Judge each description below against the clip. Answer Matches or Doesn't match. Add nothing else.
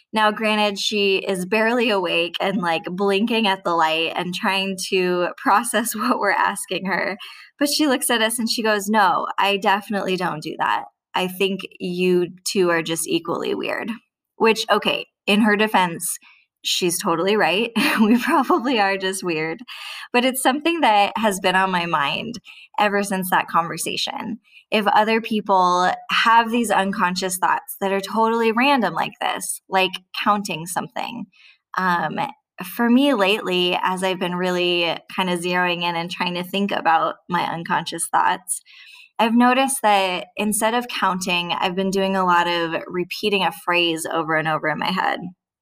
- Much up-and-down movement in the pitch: Doesn't match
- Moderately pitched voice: Doesn't match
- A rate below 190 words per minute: Matches